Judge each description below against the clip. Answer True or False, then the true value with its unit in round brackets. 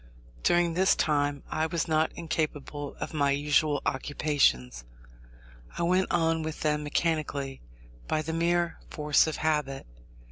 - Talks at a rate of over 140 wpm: False (135 wpm)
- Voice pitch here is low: False (155 Hz)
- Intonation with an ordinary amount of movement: False (2.2 semitones)